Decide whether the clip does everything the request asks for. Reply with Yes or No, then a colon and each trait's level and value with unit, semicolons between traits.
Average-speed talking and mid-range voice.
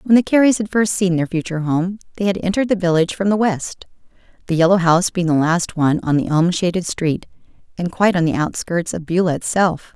No: fast, 225 wpm; medium, 180 Hz